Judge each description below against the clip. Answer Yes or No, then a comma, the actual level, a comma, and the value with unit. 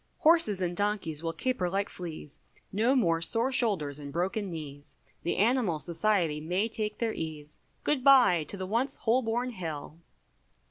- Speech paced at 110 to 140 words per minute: No, average, 155 wpm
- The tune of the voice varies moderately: No, wide, 5.9 semitones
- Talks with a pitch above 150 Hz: Yes, high, 190 Hz